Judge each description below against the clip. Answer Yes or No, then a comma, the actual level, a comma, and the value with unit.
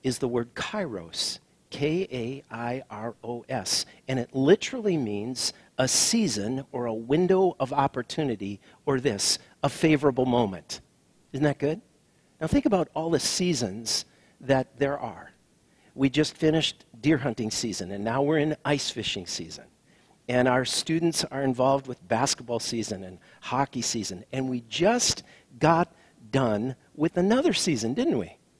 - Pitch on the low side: Yes, low, 130 Hz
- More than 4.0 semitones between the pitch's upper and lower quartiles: Yes, average, 4.5 semitones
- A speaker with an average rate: Yes, average, 150 wpm